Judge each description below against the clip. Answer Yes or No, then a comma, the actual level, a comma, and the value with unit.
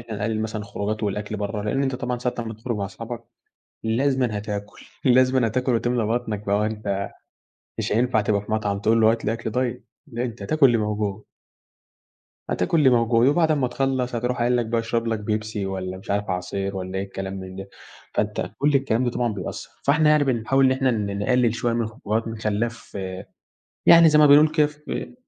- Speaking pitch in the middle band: No, low, 115 Hz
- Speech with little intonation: No, average, 3.4 semitones